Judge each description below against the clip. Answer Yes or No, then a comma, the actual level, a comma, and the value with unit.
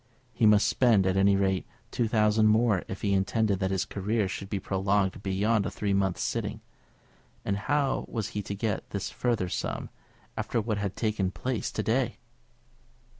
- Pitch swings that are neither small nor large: No, narrow, 2.3 semitones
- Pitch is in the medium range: No, low, 100 Hz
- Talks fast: No, average, 175 wpm